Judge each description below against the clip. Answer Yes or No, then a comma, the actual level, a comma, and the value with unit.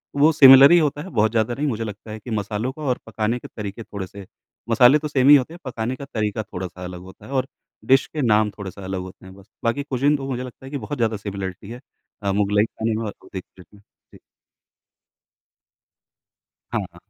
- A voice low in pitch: Yes, low, 115 Hz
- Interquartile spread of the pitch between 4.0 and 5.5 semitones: Yes, average, 4.8 semitones